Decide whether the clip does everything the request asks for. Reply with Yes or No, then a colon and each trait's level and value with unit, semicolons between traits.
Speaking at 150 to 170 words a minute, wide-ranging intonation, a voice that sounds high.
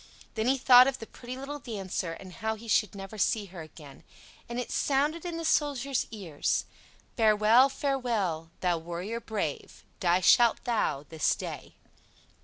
Yes: average, 160 wpm; wide, 5.9 semitones; high, 220 Hz